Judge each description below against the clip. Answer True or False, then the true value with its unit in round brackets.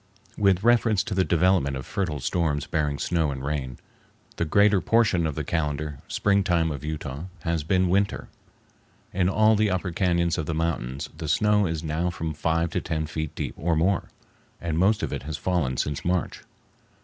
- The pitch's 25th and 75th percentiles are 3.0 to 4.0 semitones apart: True (3.5 semitones)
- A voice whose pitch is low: True (85 Hz)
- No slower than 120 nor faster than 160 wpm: False (185 wpm)